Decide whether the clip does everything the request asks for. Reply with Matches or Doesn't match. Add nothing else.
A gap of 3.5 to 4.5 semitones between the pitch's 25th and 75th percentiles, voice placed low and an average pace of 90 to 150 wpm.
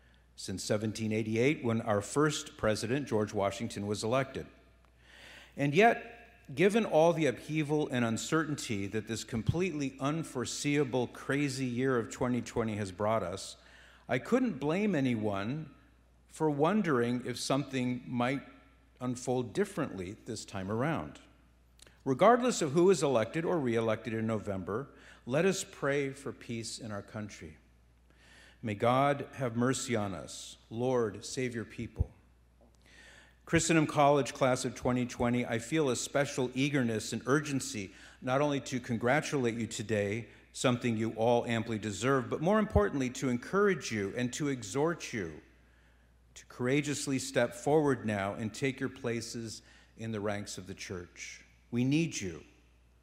Doesn't match